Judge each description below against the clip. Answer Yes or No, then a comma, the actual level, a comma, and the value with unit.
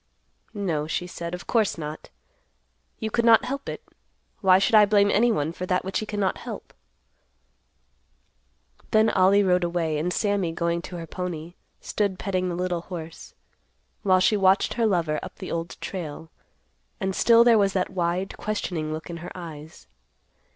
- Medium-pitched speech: Yes, medium, 180 Hz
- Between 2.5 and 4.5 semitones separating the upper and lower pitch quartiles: Yes, average, 3.2 semitones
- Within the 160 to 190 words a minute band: Yes, average, 165 wpm